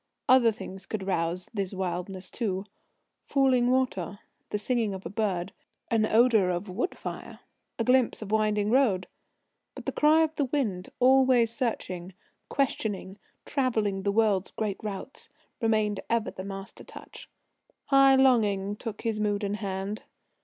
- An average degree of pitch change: Yes, average, 4.2 semitones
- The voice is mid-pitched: No, high, 210 Hz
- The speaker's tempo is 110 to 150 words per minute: Yes, average, 145 wpm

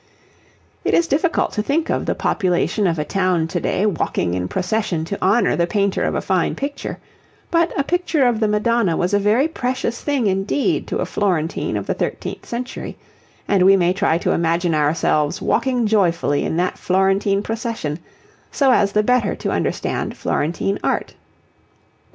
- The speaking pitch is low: No, high, 200 Hz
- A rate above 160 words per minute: Yes, average, 175 wpm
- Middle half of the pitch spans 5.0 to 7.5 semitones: Yes, average, 5.3 semitones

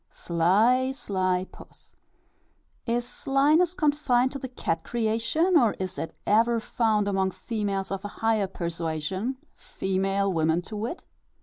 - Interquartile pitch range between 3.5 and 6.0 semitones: Yes, average, 4.7 semitones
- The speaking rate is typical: No, slow, 130 wpm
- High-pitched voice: Yes, high, 215 Hz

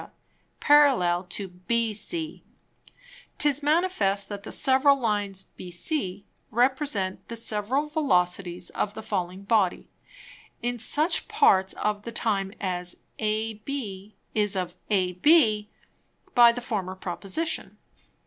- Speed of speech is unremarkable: No, slow, 110 wpm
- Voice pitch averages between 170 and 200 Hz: No, high, 210 Hz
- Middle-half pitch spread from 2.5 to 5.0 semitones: No, wide, 5.5 semitones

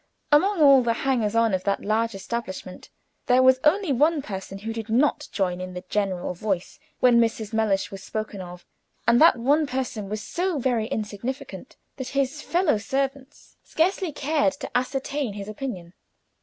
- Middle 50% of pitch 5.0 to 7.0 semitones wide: Yes, average, 5.3 semitones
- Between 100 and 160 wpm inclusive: No, average, 170 wpm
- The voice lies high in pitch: Yes, high, 235 Hz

